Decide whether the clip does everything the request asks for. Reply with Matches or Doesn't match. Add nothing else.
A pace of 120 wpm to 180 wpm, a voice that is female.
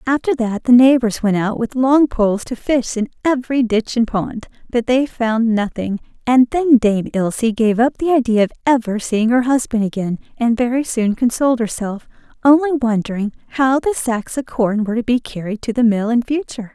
Doesn't match